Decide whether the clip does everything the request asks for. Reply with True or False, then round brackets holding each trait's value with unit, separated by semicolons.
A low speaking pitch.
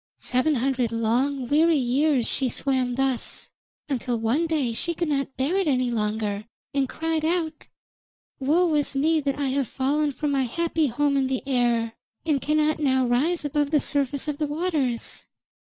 False (275 Hz)